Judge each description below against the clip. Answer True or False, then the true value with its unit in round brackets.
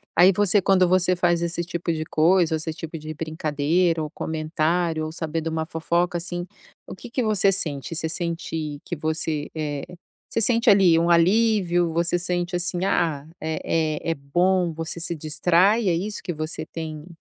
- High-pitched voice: False (170 Hz)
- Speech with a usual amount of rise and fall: False (2.2 semitones)